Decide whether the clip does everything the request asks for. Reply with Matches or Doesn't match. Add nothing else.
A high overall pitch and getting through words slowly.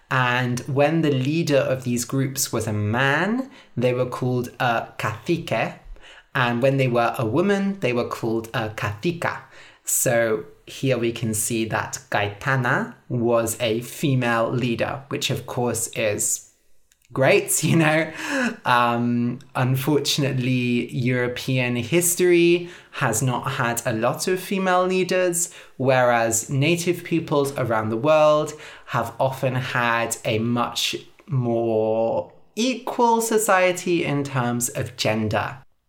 Doesn't match